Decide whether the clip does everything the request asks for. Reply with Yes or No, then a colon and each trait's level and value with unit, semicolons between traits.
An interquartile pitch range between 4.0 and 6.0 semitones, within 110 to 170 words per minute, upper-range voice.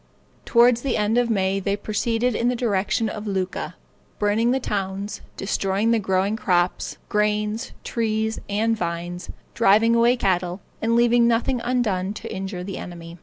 No: average, 3.4 semitones; average, 160 wpm; high, 210 Hz